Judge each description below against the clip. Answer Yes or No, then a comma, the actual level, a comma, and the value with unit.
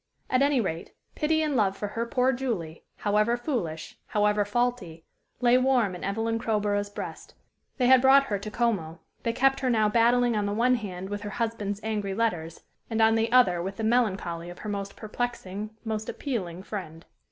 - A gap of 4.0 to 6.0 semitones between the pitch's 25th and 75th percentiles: No, average, 3.6 semitones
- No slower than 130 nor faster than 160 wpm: No, average, 185 wpm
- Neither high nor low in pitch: No, high, 215 Hz